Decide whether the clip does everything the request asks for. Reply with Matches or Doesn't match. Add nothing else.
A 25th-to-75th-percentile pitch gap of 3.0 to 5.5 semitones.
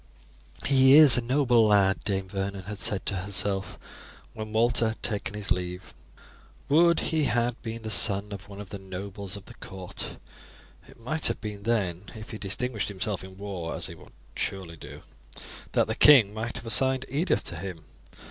Matches